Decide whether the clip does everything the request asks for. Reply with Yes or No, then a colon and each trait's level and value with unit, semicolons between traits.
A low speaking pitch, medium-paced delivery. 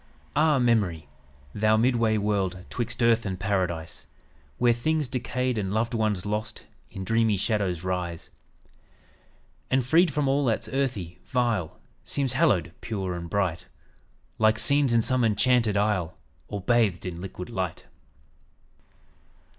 No: low, 110 Hz; slow, 130 wpm